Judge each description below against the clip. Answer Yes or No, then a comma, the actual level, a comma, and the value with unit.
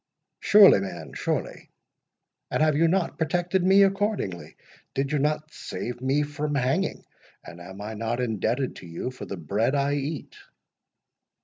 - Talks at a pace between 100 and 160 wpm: Yes, average, 150 wpm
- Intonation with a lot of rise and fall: Yes, wide, 6.2 semitones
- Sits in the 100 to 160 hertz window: Yes, medium, 140 Hz